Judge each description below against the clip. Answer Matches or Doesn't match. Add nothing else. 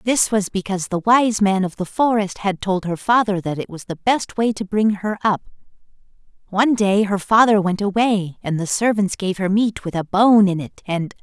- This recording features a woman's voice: Doesn't match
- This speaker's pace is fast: Matches